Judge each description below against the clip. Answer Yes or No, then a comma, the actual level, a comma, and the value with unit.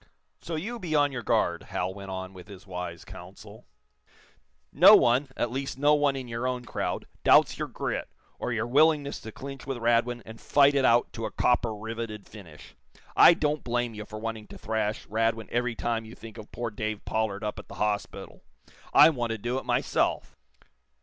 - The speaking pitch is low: Yes, low, 115 Hz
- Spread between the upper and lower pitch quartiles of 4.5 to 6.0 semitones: No, average, 3.7 semitones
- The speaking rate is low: No, average, 195 wpm